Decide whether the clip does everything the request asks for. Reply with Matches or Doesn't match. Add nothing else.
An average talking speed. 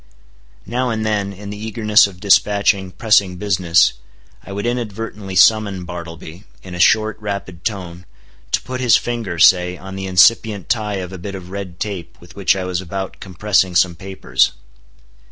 Matches